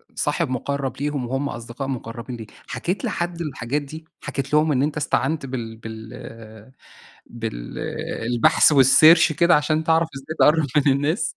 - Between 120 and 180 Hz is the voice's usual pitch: Yes, medium, 140 Hz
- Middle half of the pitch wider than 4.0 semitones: Yes, average, 4.6 semitones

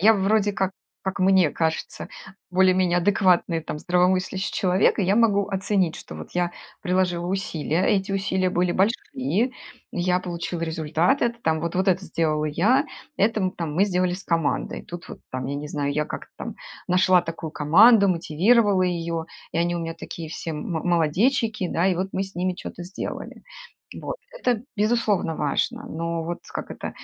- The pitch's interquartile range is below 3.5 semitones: Yes, average, 2.8 semitones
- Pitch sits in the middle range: Yes, medium, 180 Hz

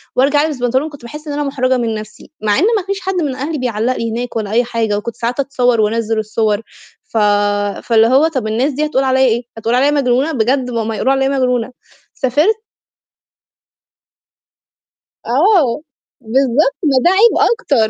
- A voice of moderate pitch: No, very high, 255 Hz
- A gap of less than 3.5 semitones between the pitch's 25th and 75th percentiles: No, average, 4.0 semitones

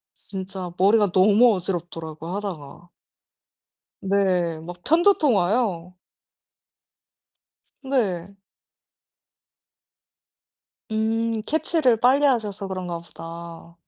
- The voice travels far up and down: No, average, 4.6 semitones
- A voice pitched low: No, high, 195 Hz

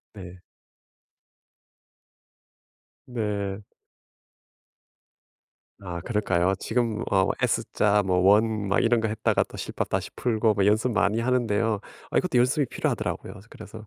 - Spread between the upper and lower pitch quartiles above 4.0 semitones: No, narrow, 2.6 semitones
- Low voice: Yes, low, 105 Hz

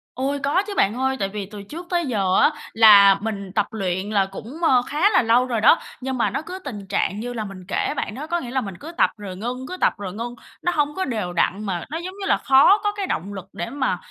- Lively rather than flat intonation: Yes, wide, 6.4 semitones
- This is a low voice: No, high, 230 Hz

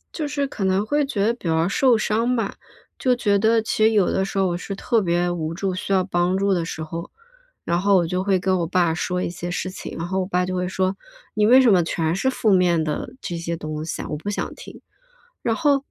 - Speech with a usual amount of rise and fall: Yes, average, 3.7 semitones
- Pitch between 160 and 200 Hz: Yes, high, 190 Hz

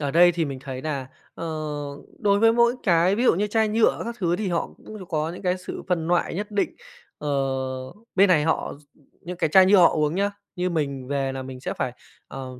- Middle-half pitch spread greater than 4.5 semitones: Yes, average, 5.2 semitones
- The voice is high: No, medium, 175 Hz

